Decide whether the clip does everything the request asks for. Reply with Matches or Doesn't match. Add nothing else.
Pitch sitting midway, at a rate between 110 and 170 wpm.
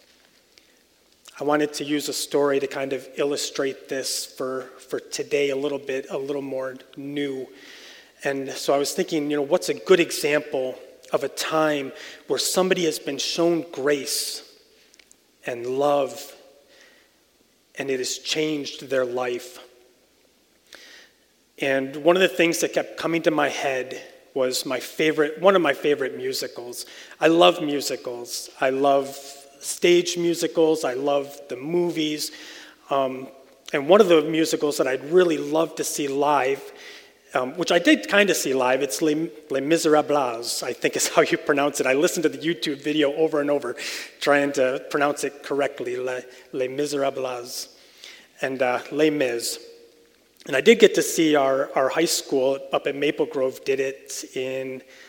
Matches